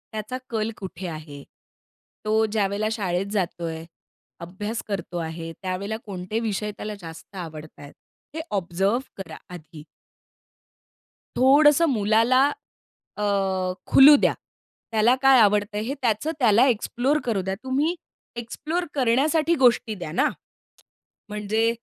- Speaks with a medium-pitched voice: No, high, 210 Hz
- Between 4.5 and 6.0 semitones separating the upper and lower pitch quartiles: Yes, average, 4.8 semitones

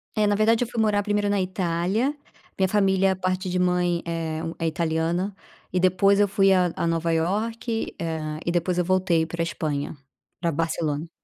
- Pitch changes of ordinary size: Yes, average, 3.2 semitones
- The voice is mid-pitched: Yes, medium, 180 Hz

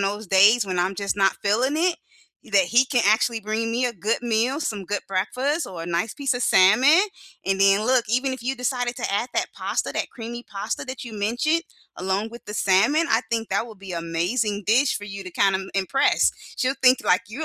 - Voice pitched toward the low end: No, high, 220 Hz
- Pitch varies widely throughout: No, average, 4.3 semitones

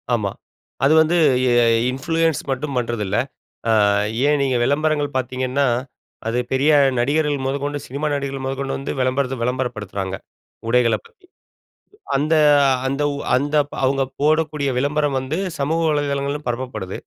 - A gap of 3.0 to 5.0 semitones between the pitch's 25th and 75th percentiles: No, narrow, 2.5 semitones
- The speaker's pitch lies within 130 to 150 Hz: Yes, low, 135 Hz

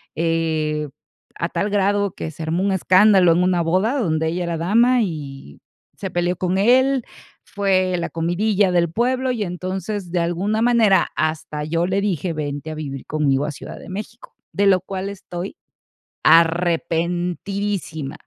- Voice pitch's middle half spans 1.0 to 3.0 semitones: No, average, 3.6 semitones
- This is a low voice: No, medium, 180 Hz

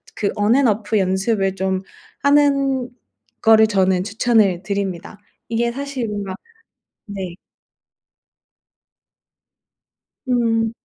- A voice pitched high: Yes, high, 215 Hz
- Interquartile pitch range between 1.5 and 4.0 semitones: Yes, average, 3.6 semitones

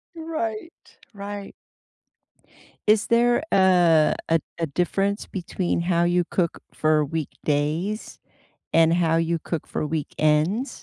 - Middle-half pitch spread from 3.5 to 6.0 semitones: Yes, average, 4.0 semitones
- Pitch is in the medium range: Yes, medium, 175 Hz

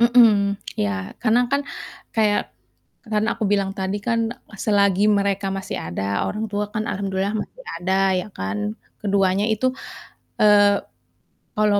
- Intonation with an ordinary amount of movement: No, narrow, 1.9 semitones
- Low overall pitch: No, high, 205 Hz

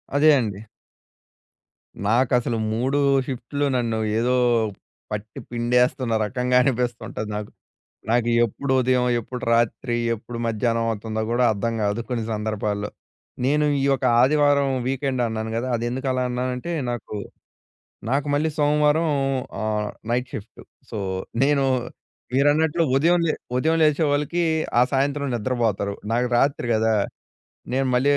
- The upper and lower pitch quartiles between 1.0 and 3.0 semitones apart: No, average, 3.7 semitones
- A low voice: Yes, low, 125 Hz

